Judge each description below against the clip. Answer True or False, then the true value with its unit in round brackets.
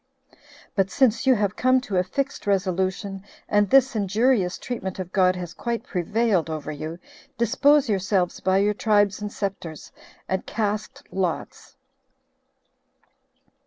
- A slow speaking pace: True (130 wpm)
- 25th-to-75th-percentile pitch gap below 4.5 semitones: True (3.7 semitones)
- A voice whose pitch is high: True (200 Hz)